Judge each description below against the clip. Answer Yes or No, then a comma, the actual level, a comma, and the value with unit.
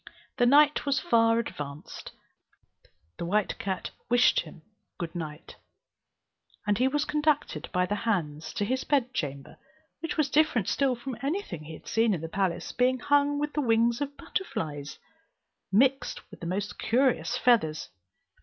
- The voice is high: Yes, high, 230 Hz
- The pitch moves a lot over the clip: Yes, wide, 7.8 semitones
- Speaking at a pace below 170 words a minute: Yes, average, 160 wpm